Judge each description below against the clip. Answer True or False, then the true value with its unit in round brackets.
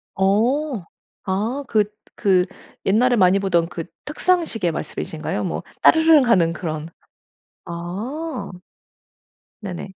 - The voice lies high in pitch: True (200 Hz)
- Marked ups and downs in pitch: True (6.4 semitones)